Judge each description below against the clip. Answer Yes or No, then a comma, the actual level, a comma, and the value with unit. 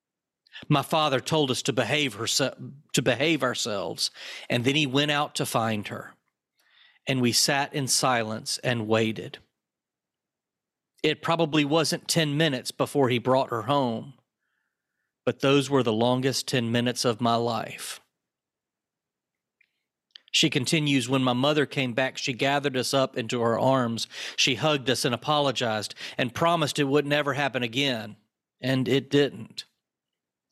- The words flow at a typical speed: Yes, average, 145 wpm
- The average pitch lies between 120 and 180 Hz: Yes, low, 135 Hz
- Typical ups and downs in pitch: Yes, average, 3.2 semitones